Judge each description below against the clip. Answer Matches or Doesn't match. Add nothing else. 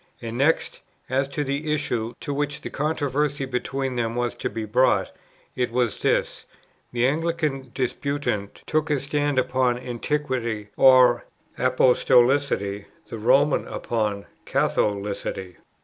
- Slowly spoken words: Matches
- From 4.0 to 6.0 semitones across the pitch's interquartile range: Doesn't match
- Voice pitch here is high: Doesn't match